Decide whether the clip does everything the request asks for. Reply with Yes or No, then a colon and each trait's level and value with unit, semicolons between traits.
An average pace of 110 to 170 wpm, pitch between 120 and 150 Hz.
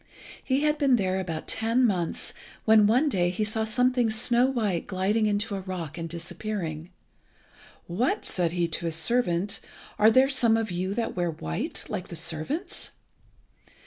No: average, 165 wpm; high, 205 Hz